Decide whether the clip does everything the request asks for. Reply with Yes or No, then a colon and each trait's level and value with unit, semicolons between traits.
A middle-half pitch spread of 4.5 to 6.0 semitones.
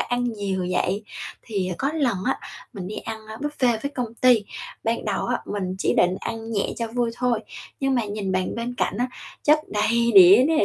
No: average, 3.5 semitones